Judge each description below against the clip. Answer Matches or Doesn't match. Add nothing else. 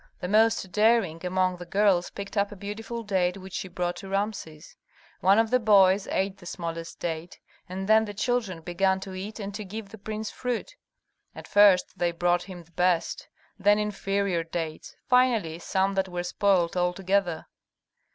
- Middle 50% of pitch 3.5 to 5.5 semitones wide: Doesn't match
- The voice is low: Doesn't match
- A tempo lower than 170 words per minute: Doesn't match